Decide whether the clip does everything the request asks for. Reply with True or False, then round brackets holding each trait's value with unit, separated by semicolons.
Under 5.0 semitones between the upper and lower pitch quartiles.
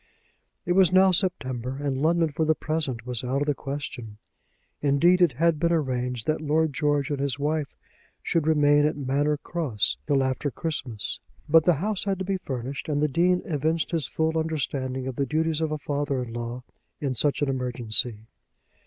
True (3.4 semitones)